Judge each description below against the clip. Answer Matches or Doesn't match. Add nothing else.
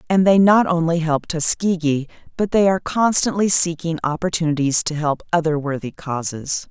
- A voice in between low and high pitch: Matches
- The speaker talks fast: Doesn't match